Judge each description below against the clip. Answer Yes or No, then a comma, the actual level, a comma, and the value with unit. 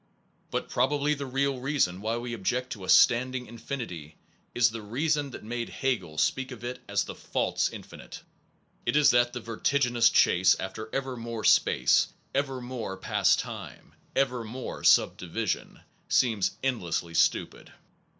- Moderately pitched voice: No, low, 120 Hz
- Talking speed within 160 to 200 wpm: No, average, 150 wpm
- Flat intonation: No, average, 3.3 semitones